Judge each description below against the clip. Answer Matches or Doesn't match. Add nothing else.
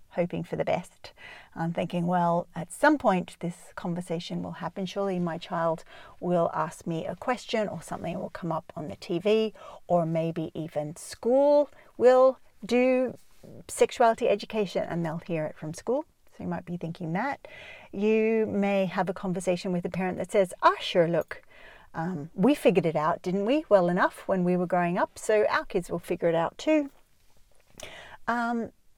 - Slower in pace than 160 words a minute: Doesn't match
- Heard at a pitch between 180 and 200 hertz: Matches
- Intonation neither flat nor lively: Matches